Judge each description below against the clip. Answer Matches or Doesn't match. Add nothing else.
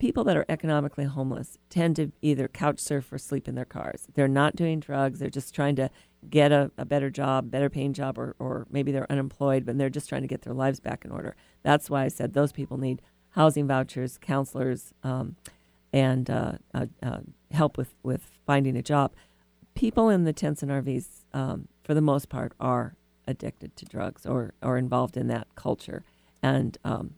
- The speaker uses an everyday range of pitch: Doesn't match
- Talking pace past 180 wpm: Matches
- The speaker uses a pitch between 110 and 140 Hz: Matches